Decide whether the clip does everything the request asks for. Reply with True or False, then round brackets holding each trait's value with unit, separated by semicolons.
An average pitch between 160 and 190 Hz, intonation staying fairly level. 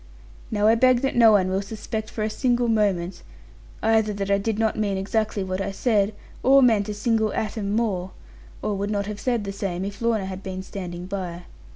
False (205 Hz; 2.3 semitones)